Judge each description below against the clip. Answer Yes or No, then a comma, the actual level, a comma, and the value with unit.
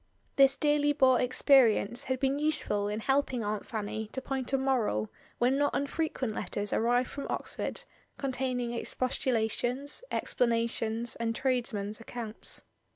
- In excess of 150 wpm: No, slow, 135 wpm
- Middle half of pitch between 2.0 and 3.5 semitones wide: Yes, average, 3.2 semitones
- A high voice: Yes, very high, 250 Hz